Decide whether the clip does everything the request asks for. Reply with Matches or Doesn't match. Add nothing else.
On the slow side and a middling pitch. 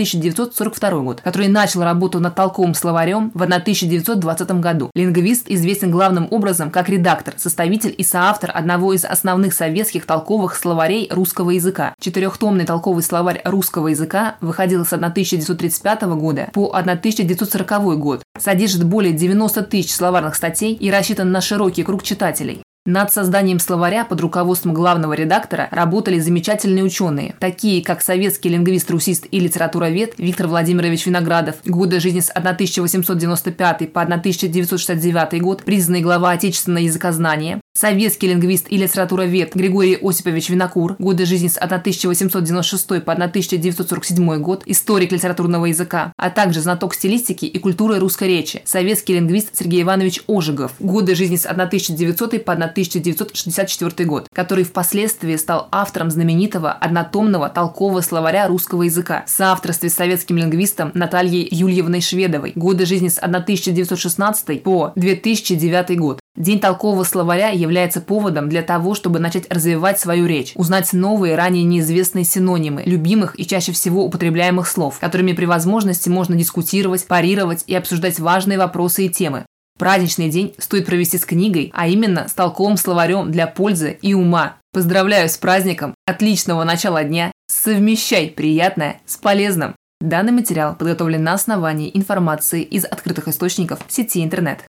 Doesn't match